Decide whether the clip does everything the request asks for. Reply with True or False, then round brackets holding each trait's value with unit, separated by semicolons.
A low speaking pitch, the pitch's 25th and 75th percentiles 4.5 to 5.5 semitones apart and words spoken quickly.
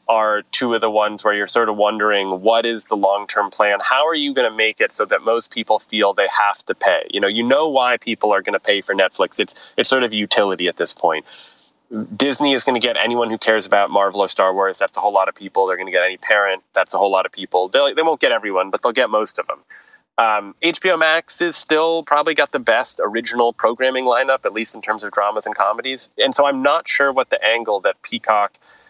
True (115 Hz; 4.8 semitones; 255 wpm)